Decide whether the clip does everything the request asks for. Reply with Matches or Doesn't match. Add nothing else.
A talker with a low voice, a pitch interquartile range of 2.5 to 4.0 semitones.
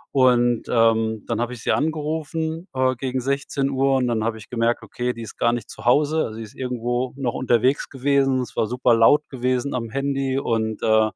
Matches